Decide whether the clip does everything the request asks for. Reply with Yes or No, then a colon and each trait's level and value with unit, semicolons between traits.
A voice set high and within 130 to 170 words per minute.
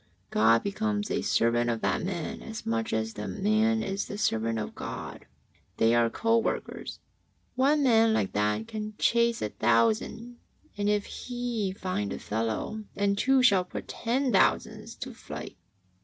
Yes: high, 200 Hz; average, 160 wpm